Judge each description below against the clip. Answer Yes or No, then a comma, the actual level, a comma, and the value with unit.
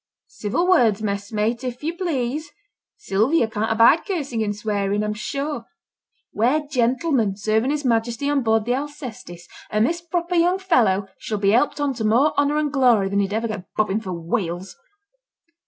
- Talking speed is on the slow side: No, average, 170 wpm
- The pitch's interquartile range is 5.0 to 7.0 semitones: Yes, wide, 5.6 semitones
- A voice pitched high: Yes, high, 235 Hz